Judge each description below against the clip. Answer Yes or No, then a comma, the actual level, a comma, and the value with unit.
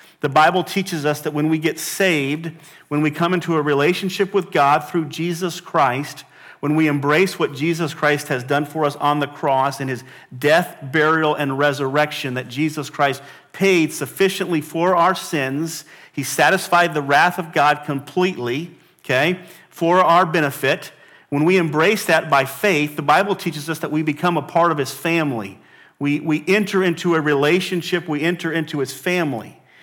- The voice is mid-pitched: Yes, medium, 155 Hz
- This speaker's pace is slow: No, average, 175 wpm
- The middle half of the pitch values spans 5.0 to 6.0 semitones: No, average, 3.0 semitones